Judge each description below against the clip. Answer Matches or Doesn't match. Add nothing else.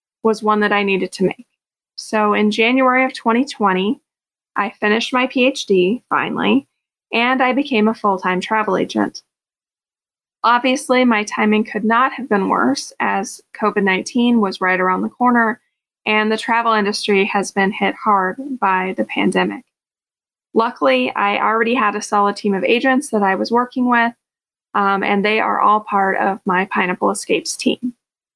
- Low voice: Doesn't match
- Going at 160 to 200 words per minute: Matches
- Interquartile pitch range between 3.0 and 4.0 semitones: Matches